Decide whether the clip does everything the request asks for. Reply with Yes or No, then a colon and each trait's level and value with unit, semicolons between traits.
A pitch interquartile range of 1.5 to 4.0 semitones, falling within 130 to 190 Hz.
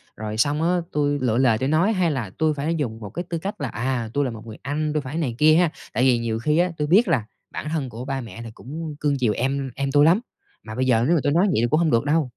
No: average, 4.7 semitones; medium, 140 Hz